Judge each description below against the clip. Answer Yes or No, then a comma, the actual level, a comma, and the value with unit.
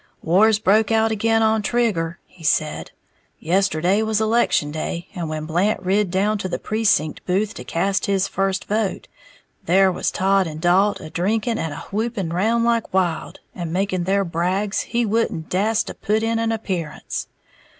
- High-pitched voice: Yes, high, 195 Hz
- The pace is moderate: Yes, average, 170 wpm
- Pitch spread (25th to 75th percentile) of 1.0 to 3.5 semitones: No, average, 3.9 semitones